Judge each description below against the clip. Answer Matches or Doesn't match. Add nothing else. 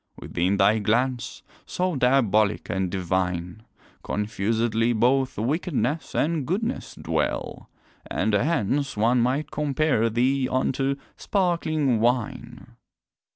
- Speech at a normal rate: Doesn't match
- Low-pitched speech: Matches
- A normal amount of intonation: Matches